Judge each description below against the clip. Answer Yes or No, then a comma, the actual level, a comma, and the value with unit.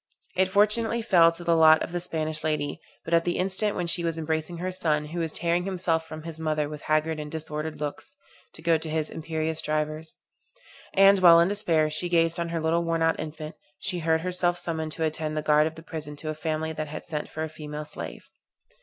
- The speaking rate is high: Yes, fast, 225 wpm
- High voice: No, medium, 160 Hz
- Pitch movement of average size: No, narrow, 1.7 semitones